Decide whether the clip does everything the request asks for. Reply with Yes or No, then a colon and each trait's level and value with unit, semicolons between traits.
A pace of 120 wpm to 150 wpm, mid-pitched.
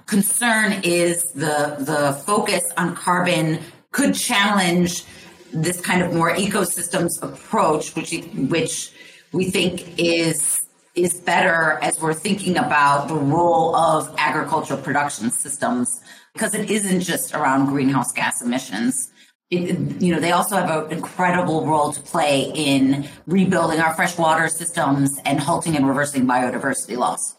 Yes: slow, 135 wpm; medium, 165 Hz